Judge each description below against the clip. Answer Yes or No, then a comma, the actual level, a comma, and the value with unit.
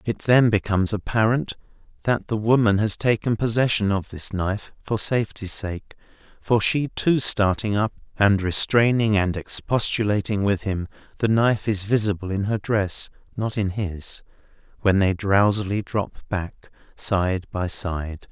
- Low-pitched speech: Yes, low, 105 Hz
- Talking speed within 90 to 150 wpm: Yes, average, 145 wpm